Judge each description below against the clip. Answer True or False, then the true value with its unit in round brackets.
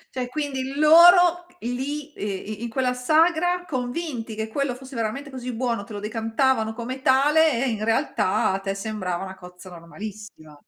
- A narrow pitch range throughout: False (4.9 semitones)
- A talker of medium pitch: False (250 Hz)